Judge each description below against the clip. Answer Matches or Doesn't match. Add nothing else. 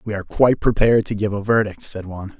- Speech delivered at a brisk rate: Matches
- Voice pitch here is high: Doesn't match